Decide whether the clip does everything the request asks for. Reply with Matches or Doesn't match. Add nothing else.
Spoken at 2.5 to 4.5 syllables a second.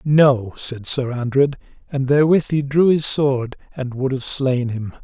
Matches